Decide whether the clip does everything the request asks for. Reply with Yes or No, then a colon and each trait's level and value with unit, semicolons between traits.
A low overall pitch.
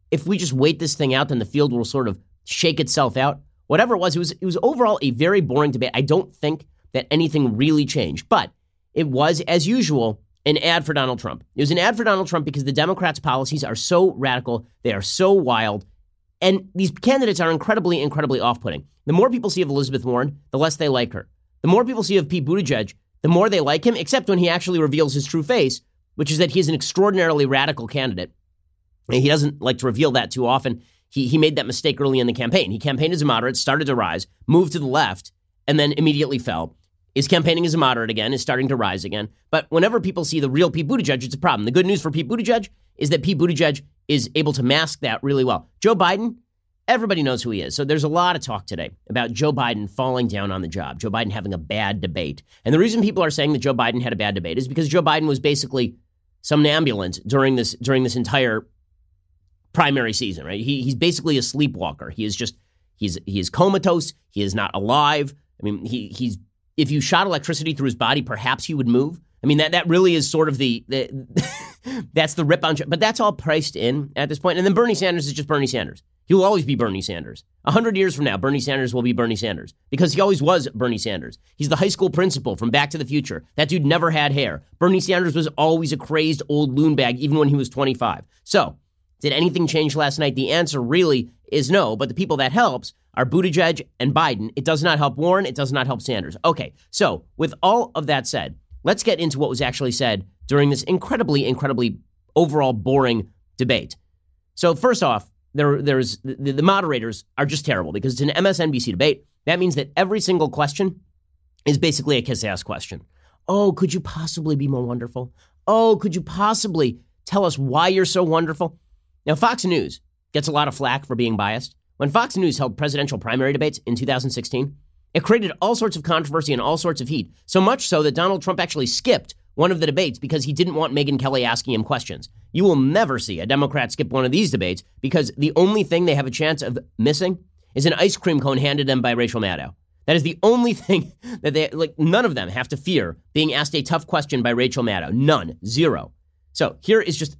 No: medium, 145 Hz